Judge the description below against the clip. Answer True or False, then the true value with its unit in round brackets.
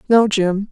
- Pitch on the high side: True (205 Hz)